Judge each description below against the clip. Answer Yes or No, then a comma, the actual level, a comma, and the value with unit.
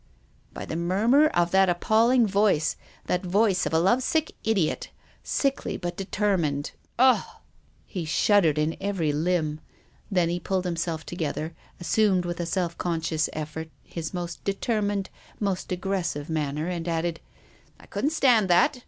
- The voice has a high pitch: No, medium, 180 Hz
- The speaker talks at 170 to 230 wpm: No, average, 160 wpm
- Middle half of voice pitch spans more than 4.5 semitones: No, average, 3.8 semitones